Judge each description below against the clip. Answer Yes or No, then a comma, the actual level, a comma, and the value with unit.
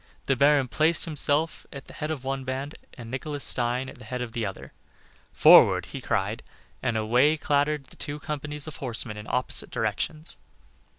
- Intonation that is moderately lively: Yes, average, 3.4 semitones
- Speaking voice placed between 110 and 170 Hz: Yes, low, 135 Hz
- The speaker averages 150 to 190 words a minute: Yes, average, 180 wpm